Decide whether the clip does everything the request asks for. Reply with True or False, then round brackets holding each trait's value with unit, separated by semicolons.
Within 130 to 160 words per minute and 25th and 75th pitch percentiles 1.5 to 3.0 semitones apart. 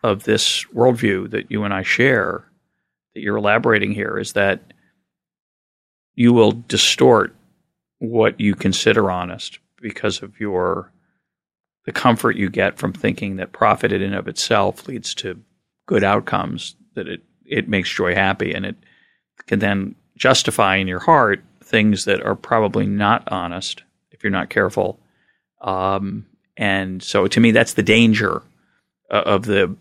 True (155 wpm; 2.7 semitones)